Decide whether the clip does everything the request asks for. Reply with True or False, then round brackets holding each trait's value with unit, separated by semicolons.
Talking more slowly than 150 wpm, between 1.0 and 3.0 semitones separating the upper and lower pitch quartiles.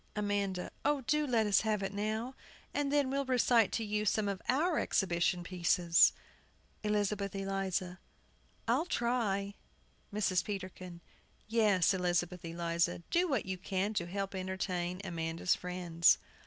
False (135 wpm; 3.5 semitones)